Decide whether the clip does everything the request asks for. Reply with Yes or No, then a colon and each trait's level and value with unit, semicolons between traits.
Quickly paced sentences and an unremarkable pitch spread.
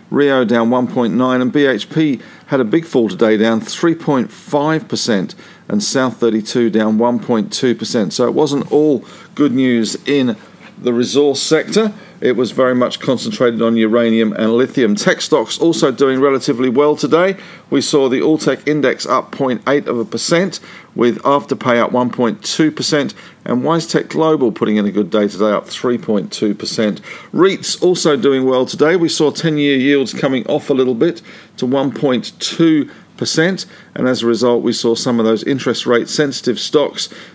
No: average, 160 wpm; average, 4.1 semitones